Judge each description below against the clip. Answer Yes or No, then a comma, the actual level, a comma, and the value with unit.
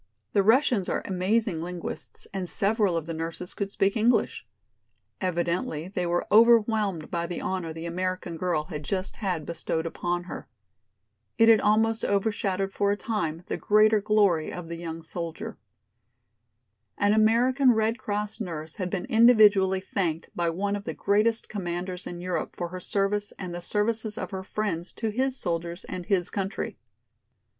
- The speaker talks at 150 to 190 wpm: Yes, average, 165 wpm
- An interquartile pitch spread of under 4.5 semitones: Yes, average, 3.6 semitones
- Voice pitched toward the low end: No, high, 190 Hz